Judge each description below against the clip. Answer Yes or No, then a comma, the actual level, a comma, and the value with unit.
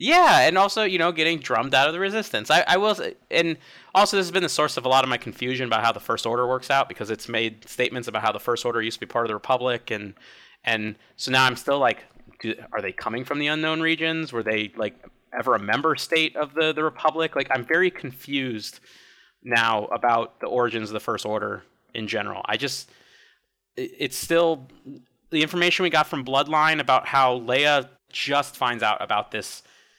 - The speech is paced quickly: Yes, fast, 215 wpm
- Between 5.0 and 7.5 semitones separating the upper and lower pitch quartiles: Yes, wide, 5.5 semitones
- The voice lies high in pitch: No, low, 135 Hz